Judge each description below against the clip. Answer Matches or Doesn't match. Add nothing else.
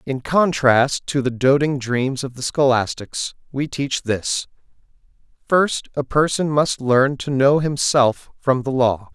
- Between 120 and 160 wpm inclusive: Matches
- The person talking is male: Matches